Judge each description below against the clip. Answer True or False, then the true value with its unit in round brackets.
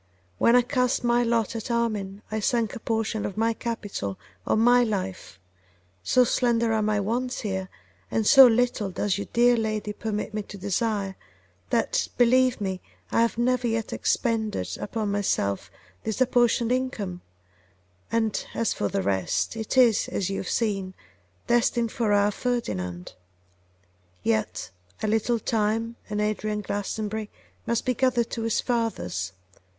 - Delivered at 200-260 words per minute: False (150 wpm)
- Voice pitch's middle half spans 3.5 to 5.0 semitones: False (2.8 semitones)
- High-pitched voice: True (220 Hz)